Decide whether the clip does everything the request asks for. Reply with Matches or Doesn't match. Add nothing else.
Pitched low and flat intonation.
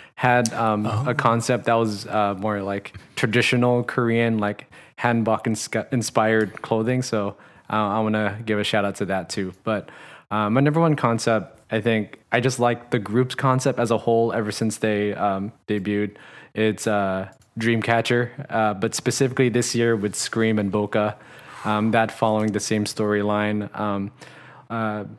Matches